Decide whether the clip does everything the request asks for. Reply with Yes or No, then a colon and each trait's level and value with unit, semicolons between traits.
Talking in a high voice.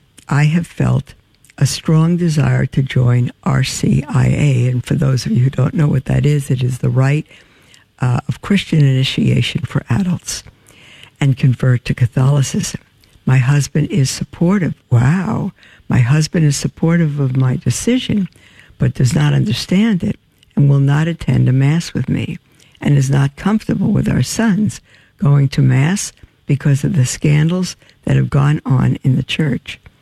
No: medium, 140 Hz